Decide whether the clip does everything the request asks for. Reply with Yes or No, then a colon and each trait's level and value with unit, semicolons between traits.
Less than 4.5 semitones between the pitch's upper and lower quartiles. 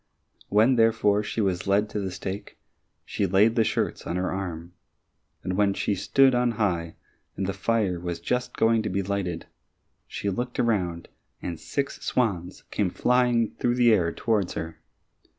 Yes: average, 4.0 semitones